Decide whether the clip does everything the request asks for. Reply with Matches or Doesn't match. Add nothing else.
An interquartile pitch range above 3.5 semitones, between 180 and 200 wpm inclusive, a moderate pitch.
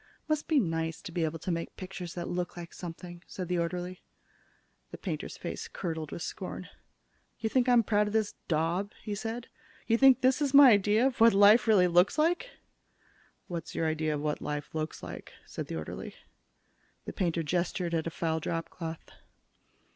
Matches